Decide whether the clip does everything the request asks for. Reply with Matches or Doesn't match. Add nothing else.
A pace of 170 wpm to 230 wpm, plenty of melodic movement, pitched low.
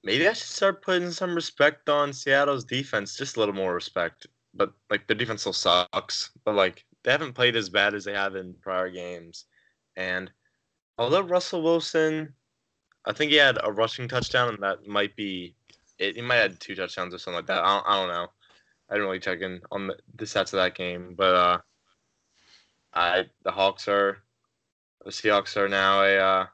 Matches